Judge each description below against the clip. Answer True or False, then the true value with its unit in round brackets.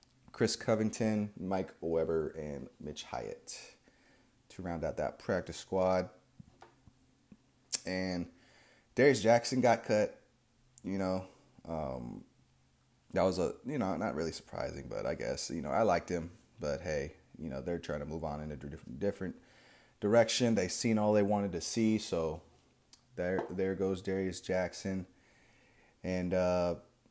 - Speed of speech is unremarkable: True (145 wpm)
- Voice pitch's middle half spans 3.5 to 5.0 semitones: True (4.4 semitones)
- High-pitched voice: False (95 Hz)